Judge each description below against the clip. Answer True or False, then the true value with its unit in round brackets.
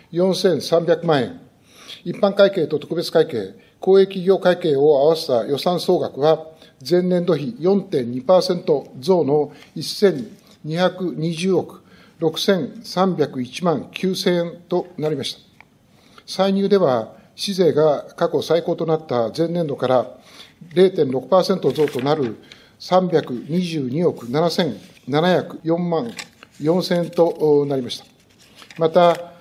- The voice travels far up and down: False (3.1 semitones)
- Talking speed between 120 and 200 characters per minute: True (155 characters per minute)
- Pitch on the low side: False (170 Hz)